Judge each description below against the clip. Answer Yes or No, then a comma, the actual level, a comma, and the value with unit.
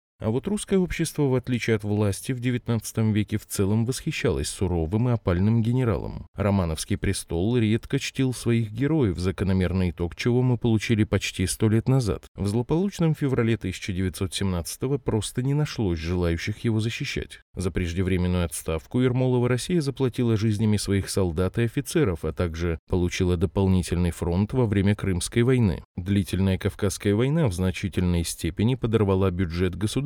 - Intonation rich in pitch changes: No, average, 4.8 semitones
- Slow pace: No, average, 145 wpm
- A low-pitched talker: Yes, low, 105 Hz